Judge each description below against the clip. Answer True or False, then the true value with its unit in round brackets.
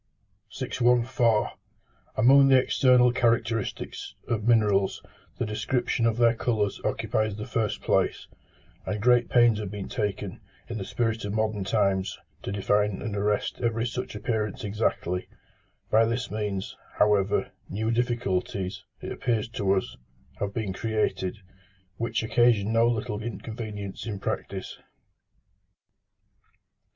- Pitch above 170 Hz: False (110 Hz)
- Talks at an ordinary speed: False (125 wpm)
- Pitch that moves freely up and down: False (2.4 semitones)